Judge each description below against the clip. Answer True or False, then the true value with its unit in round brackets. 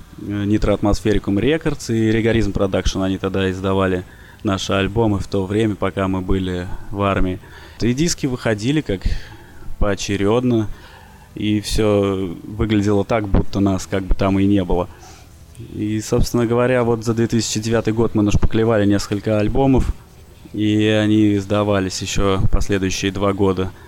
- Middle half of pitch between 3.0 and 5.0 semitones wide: False (2.4 semitones)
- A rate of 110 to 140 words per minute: True (135 wpm)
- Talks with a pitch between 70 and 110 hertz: True (100 Hz)